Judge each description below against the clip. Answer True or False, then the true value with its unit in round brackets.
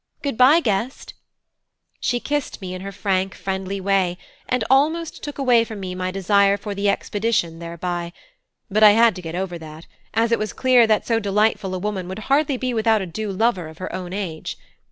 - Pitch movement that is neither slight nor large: True (3.9 semitones)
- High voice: True (200 Hz)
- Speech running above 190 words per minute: True (200 wpm)